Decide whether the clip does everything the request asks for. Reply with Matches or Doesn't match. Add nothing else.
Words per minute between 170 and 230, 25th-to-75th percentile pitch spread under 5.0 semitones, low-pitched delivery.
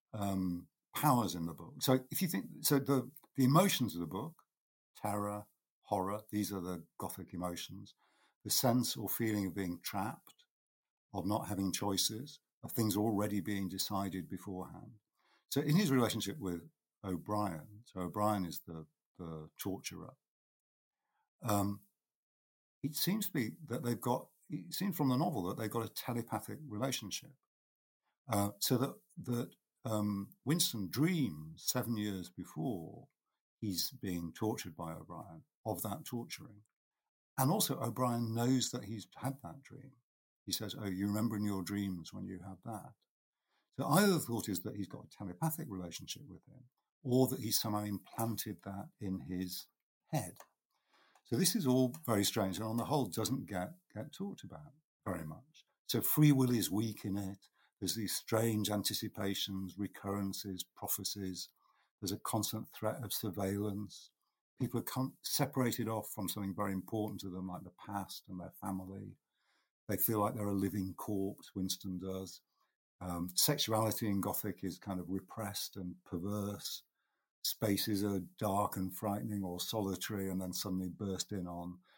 Doesn't match